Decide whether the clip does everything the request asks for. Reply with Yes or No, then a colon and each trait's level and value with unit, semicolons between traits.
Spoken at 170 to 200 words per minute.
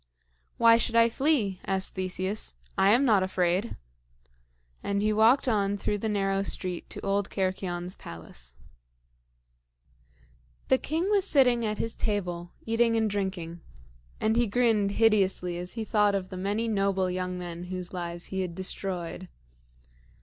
No: average, 150 wpm